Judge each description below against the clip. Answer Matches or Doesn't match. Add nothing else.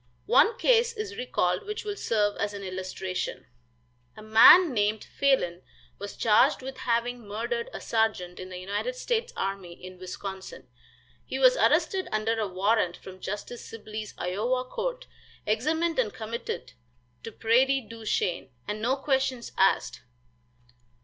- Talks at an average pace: Matches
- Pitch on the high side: Matches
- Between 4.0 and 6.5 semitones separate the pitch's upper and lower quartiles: Matches